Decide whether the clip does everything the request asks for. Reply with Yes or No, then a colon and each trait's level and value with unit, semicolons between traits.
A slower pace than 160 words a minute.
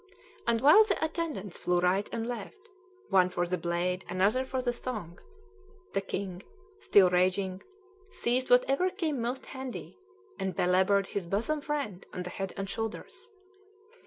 Yes: average, 150 wpm